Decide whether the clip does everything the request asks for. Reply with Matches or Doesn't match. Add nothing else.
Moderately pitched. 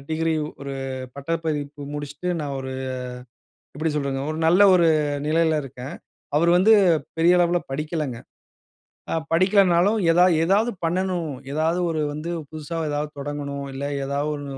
Matches